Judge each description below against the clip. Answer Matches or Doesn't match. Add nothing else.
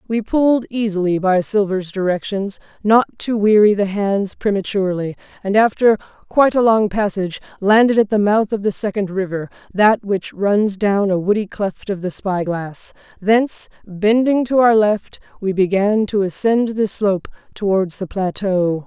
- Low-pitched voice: Doesn't match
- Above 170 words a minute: Doesn't match